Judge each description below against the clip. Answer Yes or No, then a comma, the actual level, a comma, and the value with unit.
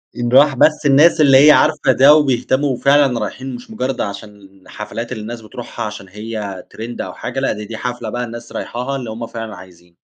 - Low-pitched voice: Yes, low, 120 Hz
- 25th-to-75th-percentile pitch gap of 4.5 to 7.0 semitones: No, average, 3.9 semitones